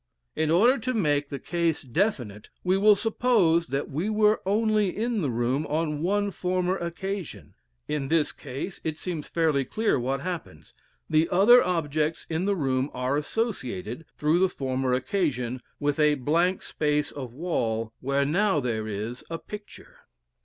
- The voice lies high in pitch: No, medium, 160 Hz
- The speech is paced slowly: No, average, 160 wpm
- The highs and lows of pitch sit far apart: Yes, wide, 5.8 semitones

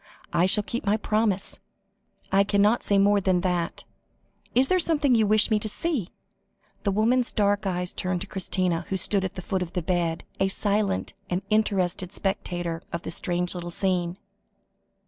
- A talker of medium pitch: No, high, 195 Hz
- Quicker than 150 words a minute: Yes, average, 175 wpm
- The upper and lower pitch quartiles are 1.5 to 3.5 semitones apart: Yes, average, 2.9 semitones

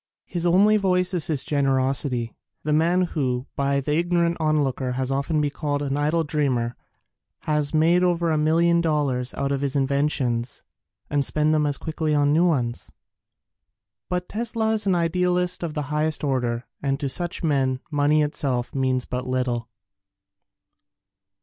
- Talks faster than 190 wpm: No, average, 160 wpm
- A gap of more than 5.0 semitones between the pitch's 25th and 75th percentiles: No, average, 3.9 semitones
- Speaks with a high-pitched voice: No, medium, 150 Hz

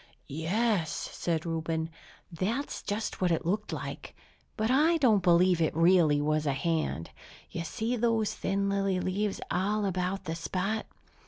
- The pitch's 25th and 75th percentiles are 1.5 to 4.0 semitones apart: No, average, 4.5 semitones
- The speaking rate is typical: Yes, average, 150 wpm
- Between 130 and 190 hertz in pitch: Yes, medium, 185 Hz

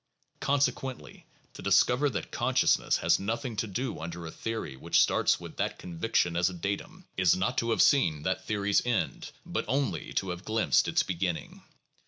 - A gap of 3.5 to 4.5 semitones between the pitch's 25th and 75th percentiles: No, average, 5.1 semitones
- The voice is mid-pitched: No, low, 100 Hz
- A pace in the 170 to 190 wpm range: Yes, average, 175 wpm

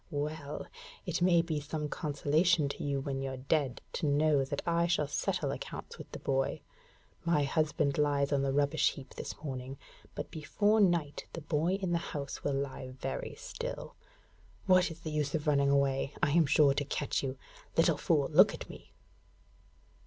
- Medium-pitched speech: Yes, medium, 150 Hz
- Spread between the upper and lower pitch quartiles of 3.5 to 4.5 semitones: No, average, 3.0 semitones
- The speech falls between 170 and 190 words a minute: Yes, average, 180 wpm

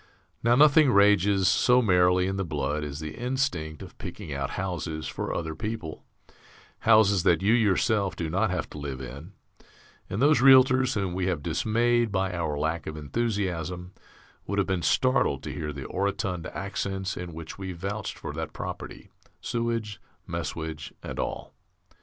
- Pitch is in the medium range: No, very low, 95 Hz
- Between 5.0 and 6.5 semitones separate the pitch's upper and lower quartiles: Yes, wide, 5.4 semitones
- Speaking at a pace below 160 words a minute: No, average, 165 wpm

